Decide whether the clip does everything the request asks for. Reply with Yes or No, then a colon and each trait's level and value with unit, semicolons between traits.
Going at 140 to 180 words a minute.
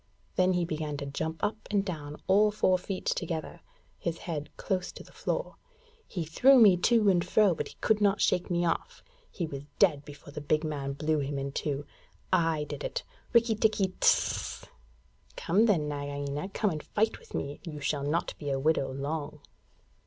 No: average, 190 wpm